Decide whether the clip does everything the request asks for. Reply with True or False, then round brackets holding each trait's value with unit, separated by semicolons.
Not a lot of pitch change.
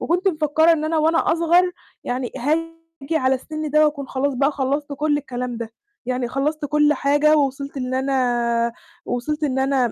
False (3.0 semitones)